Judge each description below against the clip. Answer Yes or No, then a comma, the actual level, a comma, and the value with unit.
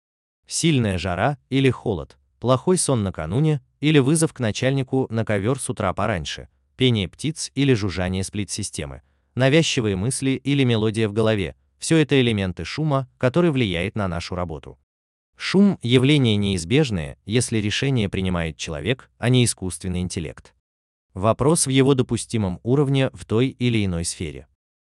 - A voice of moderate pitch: No, low, 110 Hz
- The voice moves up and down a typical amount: No, wide, 6.7 semitones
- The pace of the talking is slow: No, average, 135 wpm